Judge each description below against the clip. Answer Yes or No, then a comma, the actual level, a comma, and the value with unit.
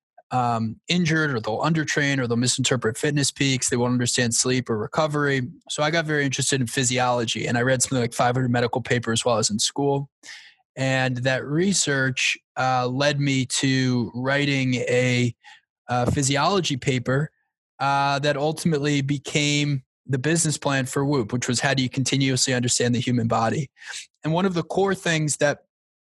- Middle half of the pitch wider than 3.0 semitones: No, average, 2.7 semitones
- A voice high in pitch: No, low, 135 Hz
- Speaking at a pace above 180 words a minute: No, average, 170 wpm